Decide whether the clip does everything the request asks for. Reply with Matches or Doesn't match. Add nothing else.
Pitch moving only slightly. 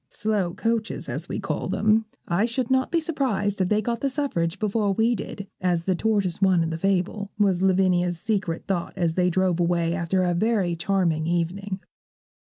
Doesn't match